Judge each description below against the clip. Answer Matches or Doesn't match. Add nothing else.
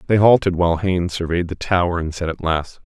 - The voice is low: Matches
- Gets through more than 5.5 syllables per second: Matches